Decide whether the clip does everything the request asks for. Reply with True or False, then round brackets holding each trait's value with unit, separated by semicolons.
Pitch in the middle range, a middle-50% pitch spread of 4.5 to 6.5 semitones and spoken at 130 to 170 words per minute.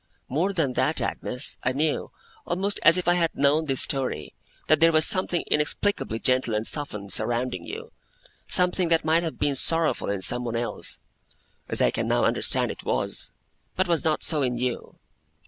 False (150 Hz; 5.1 semitones; 180 wpm)